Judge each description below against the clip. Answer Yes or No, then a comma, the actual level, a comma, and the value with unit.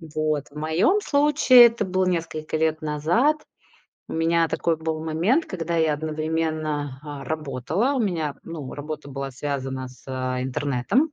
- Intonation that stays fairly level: No, average, 3.1 semitones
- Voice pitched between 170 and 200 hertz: No, medium, 155 Hz